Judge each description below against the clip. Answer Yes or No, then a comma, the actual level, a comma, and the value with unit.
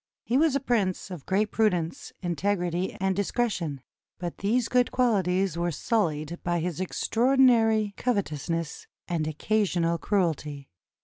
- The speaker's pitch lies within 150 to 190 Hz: Yes, medium, 185 Hz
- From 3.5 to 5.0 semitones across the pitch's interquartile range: Yes, average, 4.7 semitones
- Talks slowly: Yes, slow, 125 wpm